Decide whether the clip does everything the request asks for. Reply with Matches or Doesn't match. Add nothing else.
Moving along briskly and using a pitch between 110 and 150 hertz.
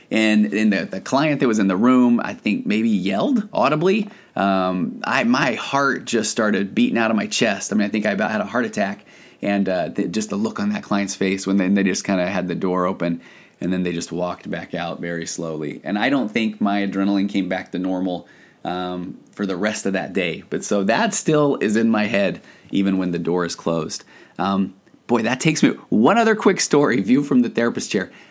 Doesn't match